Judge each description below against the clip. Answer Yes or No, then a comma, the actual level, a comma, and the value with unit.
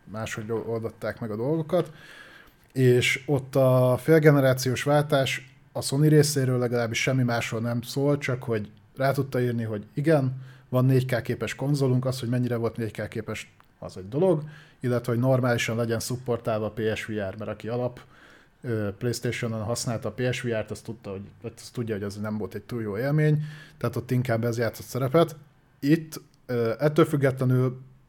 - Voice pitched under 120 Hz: No, low, 125 Hz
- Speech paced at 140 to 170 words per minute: Yes, average, 150 wpm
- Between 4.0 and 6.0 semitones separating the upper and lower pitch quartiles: No, average, 3.3 semitones